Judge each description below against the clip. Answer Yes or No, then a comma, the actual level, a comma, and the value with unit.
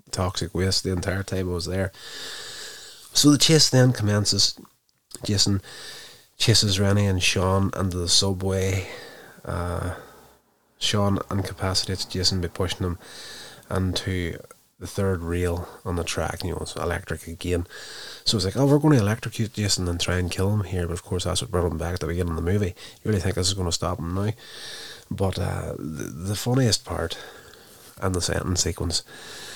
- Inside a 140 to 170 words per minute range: No, average, 180 wpm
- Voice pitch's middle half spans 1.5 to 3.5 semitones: Yes, average, 3.0 semitones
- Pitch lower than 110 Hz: Yes, very low, 95 Hz